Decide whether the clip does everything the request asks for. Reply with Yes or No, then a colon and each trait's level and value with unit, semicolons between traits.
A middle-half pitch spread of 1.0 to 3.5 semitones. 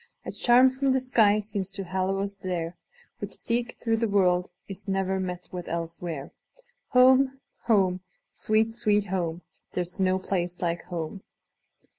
No: average, 4.3 semitones